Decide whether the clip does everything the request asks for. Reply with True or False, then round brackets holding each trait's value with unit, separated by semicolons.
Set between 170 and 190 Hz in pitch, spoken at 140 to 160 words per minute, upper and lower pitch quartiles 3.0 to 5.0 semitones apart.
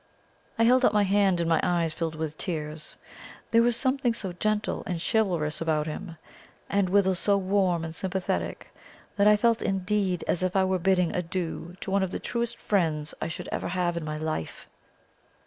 False (185 Hz; 190 wpm; 3.6 semitones)